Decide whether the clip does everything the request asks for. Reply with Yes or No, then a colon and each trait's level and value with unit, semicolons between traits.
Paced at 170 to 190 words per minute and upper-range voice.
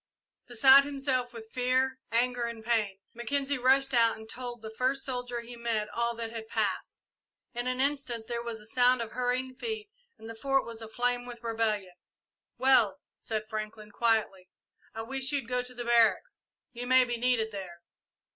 Yes: average, 175 wpm; high, 240 Hz